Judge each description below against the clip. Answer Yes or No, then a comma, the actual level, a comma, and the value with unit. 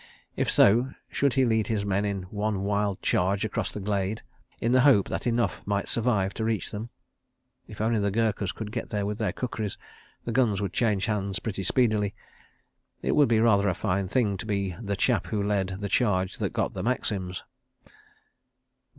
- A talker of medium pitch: No, low, 105 Hz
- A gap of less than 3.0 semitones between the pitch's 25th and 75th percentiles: Yes, narrow, 2.4 semitones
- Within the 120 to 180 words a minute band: No, average, 190 wpm